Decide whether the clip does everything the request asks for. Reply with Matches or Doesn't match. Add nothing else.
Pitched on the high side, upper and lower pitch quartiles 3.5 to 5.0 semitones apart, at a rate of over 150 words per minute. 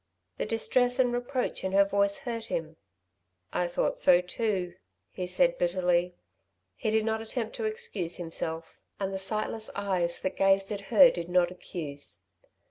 Matches